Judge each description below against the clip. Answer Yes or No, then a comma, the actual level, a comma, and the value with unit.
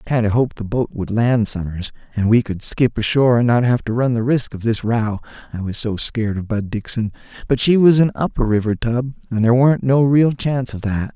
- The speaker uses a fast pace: Yes, fast, 250 wpm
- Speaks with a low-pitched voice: Yes, low, 120 Hz